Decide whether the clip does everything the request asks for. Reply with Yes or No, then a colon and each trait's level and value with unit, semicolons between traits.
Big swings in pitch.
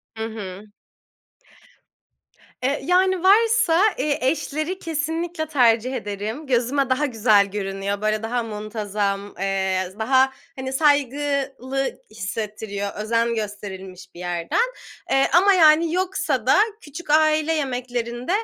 Yes: wide, 6.6 semitones